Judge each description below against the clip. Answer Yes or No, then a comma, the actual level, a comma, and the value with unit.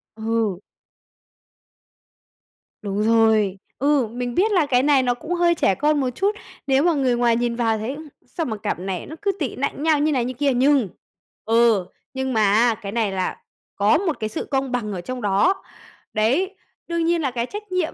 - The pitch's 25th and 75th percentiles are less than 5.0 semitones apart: No, average, 5.3 semitones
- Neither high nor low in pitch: No, very high, 250 Hz